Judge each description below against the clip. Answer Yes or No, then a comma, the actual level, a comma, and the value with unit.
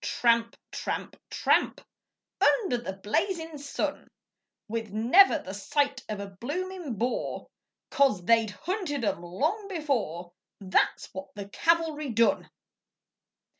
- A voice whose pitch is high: Yes, high, 245 Hz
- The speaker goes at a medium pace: No, slow, 115 wpm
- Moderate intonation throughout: No, wide, 7.7 semitones